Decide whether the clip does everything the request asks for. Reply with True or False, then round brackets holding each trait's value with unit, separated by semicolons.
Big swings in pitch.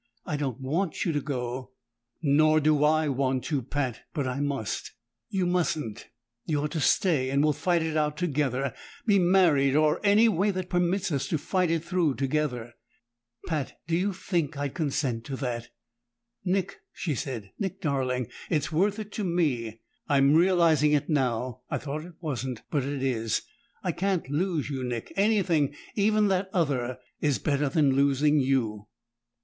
False (4.7 semitones)